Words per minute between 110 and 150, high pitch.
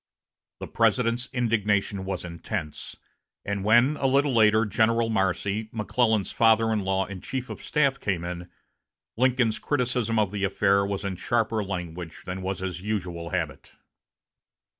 No: average, 145 wpm; low, 105 Hz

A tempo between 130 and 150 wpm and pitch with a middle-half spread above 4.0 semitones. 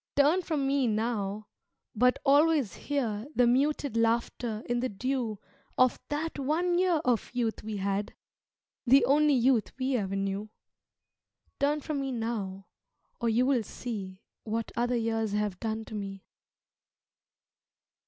Yes: average, 140 wpm; average, 4.4 semitones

